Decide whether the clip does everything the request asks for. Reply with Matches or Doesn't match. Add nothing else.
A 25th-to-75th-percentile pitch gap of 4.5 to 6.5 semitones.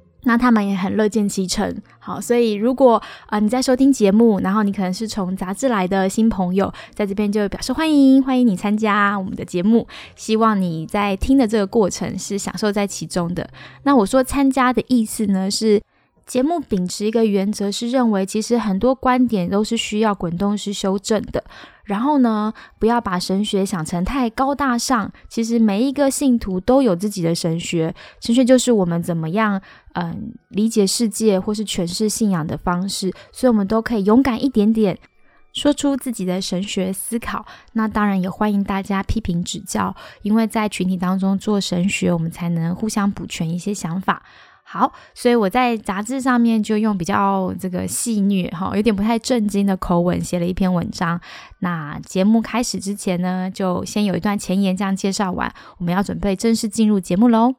Doesn't match